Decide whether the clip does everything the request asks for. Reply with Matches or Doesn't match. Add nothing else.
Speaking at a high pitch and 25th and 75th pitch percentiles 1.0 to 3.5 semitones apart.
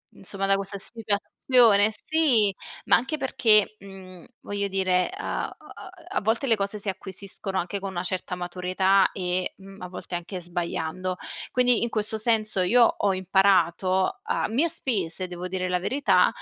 Matches